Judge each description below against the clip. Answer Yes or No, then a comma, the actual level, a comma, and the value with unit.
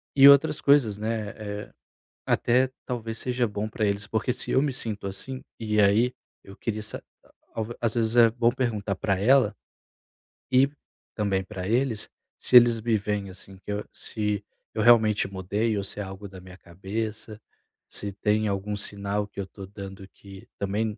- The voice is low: Yes, low, 105 Hz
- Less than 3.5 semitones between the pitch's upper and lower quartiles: Yes, average, 2.8 semitones